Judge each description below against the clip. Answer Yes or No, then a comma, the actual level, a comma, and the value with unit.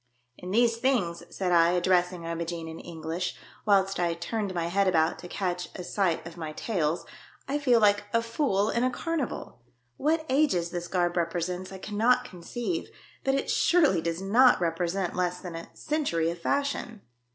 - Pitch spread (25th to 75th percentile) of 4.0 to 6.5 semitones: Yes, average, 5.3 semitones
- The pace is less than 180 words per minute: No, average, 185 wpm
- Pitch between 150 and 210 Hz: Yes, medium, 185 Hz